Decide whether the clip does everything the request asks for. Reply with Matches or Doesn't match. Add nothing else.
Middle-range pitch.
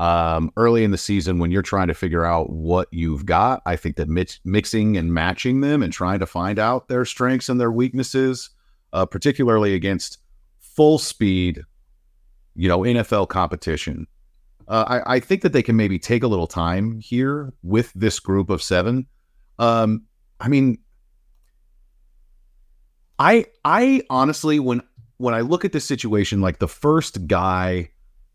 Doesn't match